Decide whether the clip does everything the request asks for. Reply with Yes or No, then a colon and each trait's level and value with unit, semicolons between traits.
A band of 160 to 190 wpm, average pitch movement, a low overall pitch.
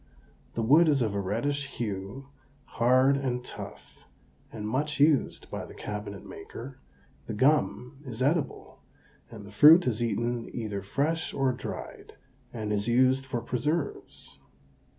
No: average, 140 wpm; average, 4.1 semitones; low, 125 Hz